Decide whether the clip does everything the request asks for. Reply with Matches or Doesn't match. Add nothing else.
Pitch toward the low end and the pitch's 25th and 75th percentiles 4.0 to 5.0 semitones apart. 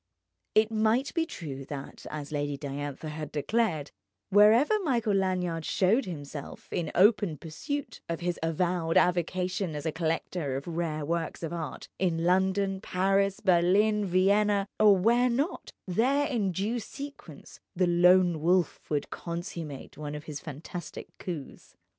Doesn't match